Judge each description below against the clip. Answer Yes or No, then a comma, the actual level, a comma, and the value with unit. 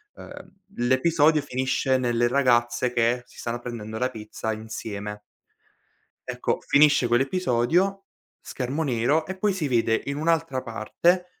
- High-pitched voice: No, low, 130 Hz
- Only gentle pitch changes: No, average, 4.8 semitones